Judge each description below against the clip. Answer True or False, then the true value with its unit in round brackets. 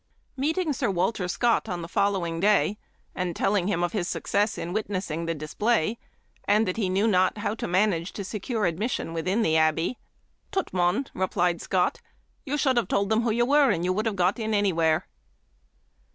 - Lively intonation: False (4.0 semitones)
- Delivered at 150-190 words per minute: False (200 wpm)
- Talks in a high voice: True (200 Hz)